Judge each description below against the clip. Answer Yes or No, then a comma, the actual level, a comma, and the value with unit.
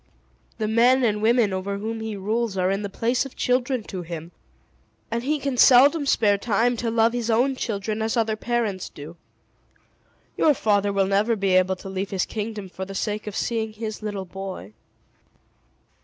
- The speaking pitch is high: Yes, high, 215 Hz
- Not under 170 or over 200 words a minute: Yes, average, 185 wpm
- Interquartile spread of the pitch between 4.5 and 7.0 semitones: No, average, 3.1 semitones